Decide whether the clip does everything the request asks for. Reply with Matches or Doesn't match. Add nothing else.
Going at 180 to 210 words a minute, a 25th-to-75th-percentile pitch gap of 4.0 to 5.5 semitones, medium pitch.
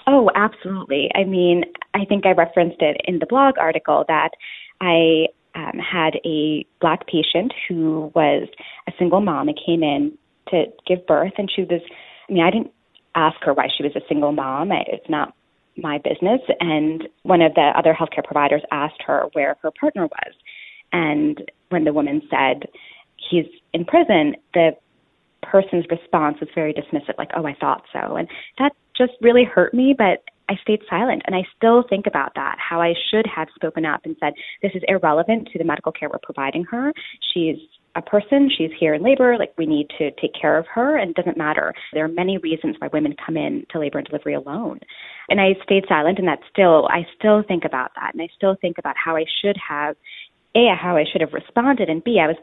Matches